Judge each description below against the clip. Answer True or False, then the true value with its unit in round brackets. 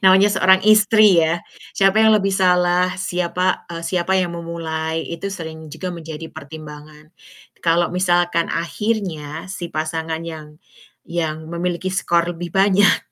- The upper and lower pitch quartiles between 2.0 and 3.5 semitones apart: True (2.7 semitones)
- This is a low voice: False (170 Hz)